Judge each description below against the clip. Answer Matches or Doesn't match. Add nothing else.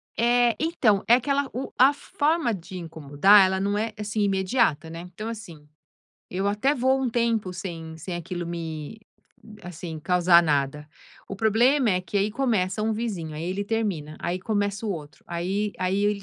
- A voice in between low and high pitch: Doesn't match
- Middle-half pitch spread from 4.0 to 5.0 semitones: Matches